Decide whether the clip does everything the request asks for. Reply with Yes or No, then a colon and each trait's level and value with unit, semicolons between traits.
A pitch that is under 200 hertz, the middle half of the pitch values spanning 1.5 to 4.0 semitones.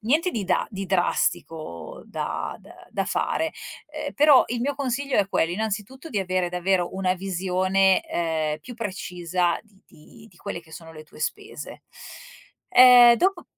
No: high, 190 Hz; average, 5.3 semitones